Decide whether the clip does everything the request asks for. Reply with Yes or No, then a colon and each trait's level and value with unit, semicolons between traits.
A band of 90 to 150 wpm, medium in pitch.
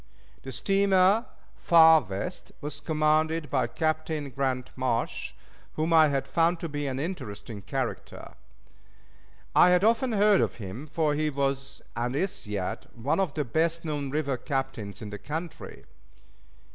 Yes: average, 145 wpm; medium, 150 Hz